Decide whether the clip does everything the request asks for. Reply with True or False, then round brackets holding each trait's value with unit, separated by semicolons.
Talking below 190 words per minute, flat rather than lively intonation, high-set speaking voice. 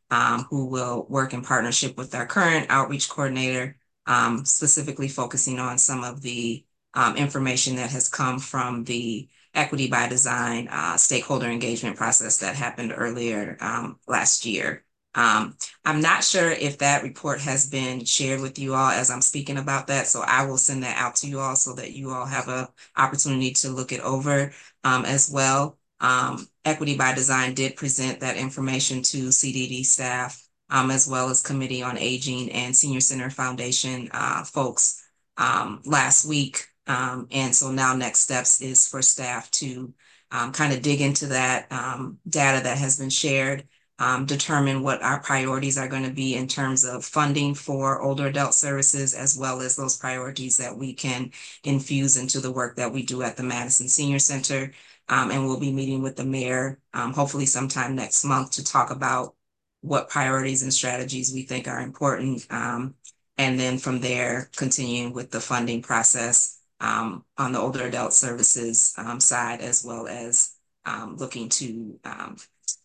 False (175 wpm; 1.5 semitones; 130 Hz)